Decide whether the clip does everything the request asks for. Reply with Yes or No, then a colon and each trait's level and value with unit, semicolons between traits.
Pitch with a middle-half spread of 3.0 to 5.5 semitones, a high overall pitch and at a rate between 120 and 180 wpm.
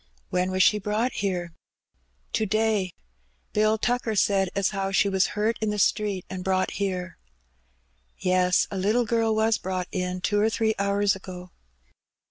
No: narrow, 2.6 semitones; high, 200 Hz; average, 160 wpm